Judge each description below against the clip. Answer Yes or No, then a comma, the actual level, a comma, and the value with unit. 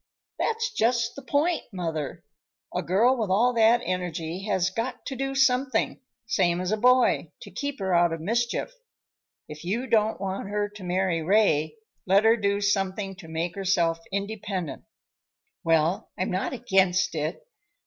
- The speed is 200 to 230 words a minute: No, average, 160 wpm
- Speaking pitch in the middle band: No, high, 195 Hz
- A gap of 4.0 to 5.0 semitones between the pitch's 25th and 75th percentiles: Yes, average, 4.7 semitones